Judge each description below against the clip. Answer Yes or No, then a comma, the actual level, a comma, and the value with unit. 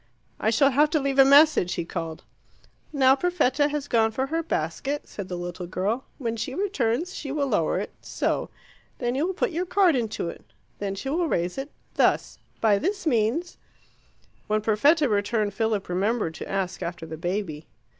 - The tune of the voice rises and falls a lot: Yes, wide, 7.0 semitones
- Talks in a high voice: Yes, high, 235 Hz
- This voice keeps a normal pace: Yes, average, 185 wpm